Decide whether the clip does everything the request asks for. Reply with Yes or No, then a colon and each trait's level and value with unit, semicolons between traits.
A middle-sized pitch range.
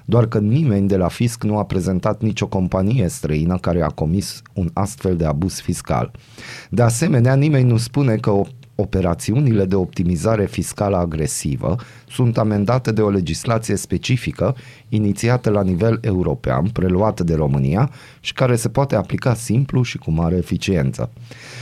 Yes: average, 5.0 semitones